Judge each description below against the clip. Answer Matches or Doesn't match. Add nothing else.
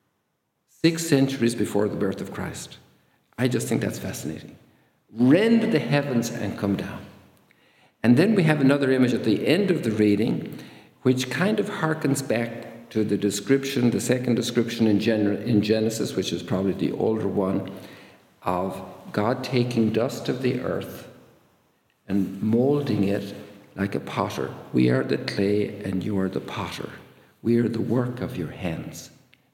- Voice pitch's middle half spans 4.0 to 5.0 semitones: Matches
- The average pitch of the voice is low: Matches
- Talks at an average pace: Matches